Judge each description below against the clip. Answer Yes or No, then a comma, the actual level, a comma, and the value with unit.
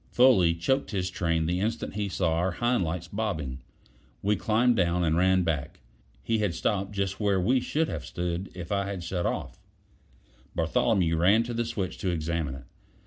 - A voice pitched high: No, very low, 95 Hz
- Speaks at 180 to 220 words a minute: Yes, average, 185 wpm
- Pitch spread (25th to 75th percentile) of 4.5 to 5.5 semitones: No, average, 3.8 semitones